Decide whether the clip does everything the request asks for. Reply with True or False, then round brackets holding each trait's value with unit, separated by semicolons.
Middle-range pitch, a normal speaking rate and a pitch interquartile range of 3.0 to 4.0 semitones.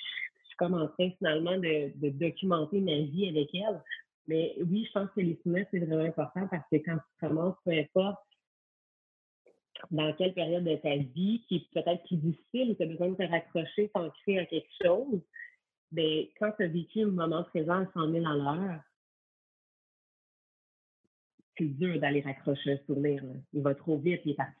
True (170 Hz; 180 wpm; 3.4 semitones)